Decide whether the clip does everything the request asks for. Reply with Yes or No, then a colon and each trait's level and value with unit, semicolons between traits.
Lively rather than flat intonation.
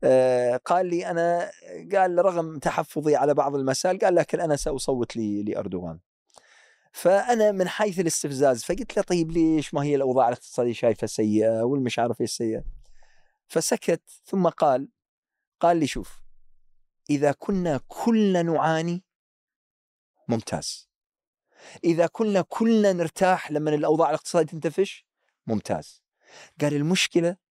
Yes: wide, 5.8 semitones